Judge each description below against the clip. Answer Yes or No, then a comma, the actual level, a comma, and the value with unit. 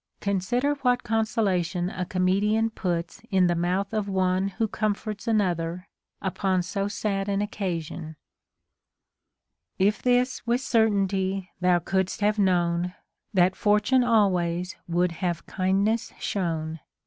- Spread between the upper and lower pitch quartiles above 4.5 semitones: No, average, 2.9 semitones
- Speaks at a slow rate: Yes, slow, 125 wpm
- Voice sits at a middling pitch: No, high, 195 Hz